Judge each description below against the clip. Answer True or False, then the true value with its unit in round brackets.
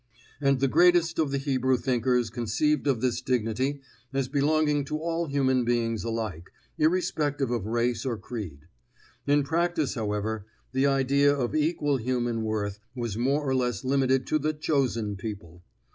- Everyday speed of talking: True (155 wpm)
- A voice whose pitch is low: True (130 Hz)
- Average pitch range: True (3.8 semitones)